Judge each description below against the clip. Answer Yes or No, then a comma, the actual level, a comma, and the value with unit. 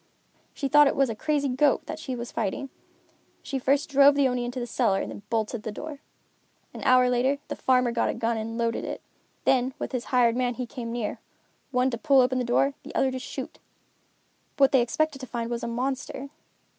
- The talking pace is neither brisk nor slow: No, fast, 220 wpm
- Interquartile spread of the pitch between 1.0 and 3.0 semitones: Yes, narrow, 2.5 semitones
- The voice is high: Yes, very high, 255 Hz